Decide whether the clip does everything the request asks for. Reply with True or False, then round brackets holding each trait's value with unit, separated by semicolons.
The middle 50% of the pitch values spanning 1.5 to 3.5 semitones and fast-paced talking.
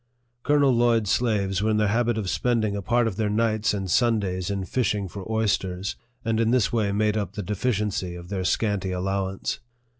False (2.8 semitones; 190 wpm)